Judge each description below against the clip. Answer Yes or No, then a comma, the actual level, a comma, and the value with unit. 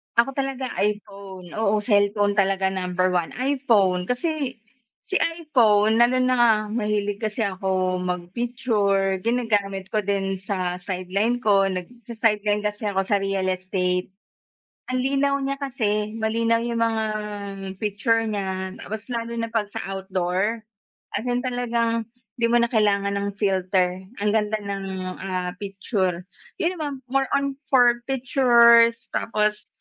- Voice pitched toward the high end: Yes, high, 210 Hz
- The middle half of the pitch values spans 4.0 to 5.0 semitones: No, average, 3.6 semitones